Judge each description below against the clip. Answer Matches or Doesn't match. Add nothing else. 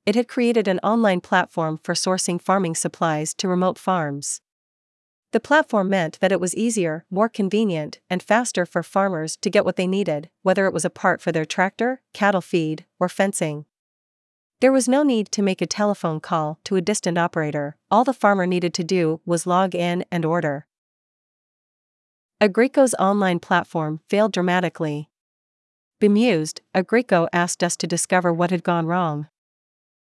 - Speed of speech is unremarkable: Matches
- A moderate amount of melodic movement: Matches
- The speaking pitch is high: Doesn't match